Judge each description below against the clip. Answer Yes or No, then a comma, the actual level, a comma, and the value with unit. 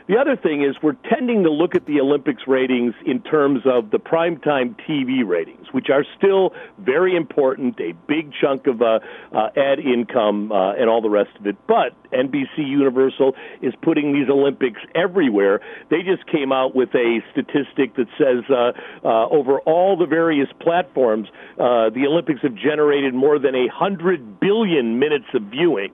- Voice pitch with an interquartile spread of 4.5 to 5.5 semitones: Yes, average, 5.1 semitones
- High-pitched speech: No, medium, 140 Hz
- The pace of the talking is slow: No, average, 175 wpm